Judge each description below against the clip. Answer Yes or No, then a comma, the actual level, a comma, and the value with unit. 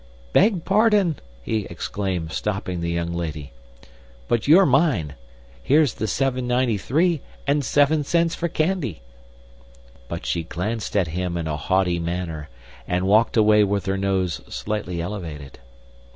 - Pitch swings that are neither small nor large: No, wide, 8.5 semitones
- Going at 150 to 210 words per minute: No, average, 140 wpm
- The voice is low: Yes, low, 100 Hz